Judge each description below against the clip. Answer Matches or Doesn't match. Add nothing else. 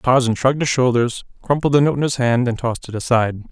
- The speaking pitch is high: Doesn't match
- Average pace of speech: Doesn't match